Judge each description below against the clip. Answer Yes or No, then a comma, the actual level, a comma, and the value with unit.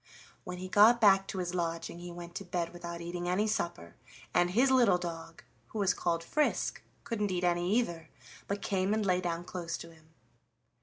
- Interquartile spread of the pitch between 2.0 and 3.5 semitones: Yes, average, 2.7 semitones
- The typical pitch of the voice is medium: Yes, medium, 180 Hz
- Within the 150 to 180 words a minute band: No, average, 195 wpm